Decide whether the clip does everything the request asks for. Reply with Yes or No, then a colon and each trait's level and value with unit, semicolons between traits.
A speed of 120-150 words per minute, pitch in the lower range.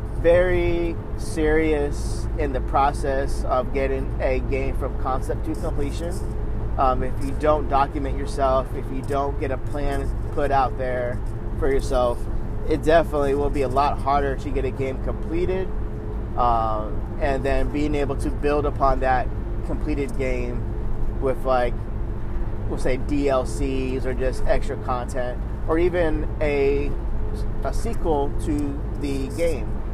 Yes: average, 140 wpm; low, 130 Hz